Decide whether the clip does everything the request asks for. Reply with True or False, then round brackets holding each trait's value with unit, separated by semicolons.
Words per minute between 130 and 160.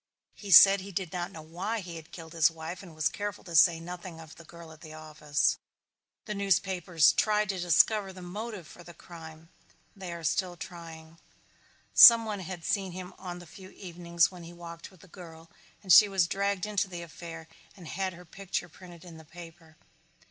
False (200 wpm)